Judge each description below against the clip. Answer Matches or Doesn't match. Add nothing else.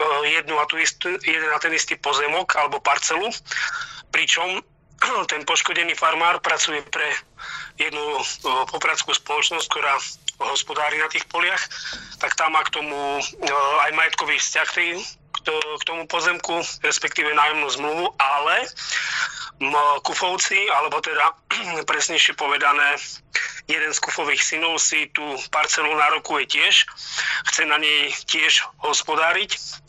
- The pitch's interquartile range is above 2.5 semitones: Doesn't match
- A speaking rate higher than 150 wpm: Doesn't match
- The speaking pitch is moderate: Matches